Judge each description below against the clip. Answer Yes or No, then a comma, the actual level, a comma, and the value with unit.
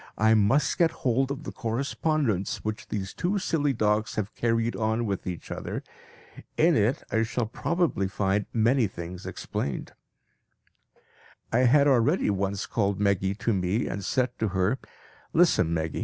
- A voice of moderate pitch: No, low, 110 Hz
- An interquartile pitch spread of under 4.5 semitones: No, average, 5.1 semitones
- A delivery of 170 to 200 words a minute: No, average, 155 wpm